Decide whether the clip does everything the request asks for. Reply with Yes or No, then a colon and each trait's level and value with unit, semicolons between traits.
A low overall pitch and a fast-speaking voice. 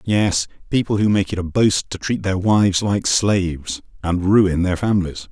No: very low, 95 Hz; average, 190 wpm